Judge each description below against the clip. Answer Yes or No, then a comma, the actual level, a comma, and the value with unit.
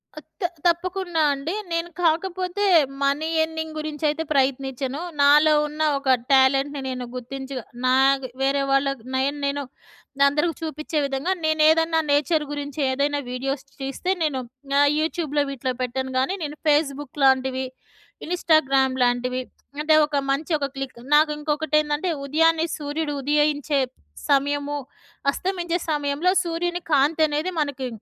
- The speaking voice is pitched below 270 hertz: No, very high, 290 Hz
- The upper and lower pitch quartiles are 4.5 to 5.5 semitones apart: No, average, 2.7 semitones